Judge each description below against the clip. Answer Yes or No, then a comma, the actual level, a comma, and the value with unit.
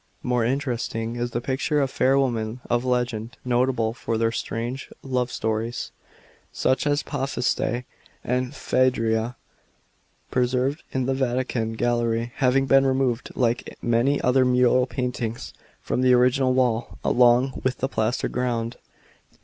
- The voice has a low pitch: Yes, low, 125 Hz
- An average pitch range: No, narrow, 1.8 semitones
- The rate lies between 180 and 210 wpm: No, average, 140 wpm